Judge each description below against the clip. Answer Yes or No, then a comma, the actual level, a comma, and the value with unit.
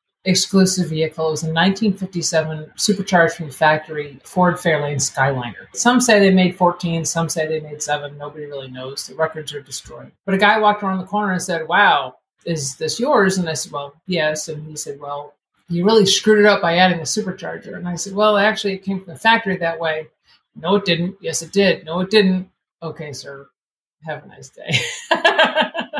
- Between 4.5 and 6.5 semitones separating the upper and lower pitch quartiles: No, average, 3.9 semitones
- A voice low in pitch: No, medium, 170 Hz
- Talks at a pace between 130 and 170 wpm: No, fast, 205 wpm